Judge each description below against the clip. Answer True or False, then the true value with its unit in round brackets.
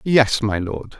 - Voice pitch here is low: True (110 Hz)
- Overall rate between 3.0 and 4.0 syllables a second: True (3.4 syllables/s)